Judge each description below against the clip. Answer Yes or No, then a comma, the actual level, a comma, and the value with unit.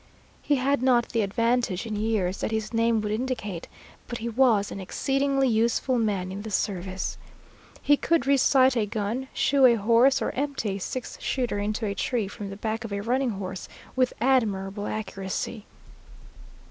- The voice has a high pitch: Yes, high, 225 Hz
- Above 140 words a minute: Yes, average, 170 wpm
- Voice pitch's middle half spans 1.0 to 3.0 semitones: No, average, 4.1 semitones